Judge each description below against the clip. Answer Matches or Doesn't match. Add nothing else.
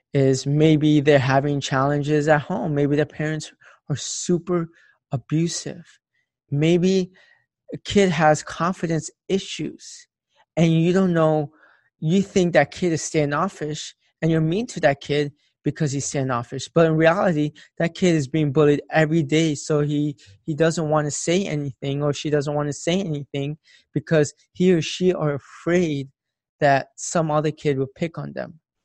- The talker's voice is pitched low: Doesn't match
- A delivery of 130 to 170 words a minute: Matches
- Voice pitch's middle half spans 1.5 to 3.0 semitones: Matches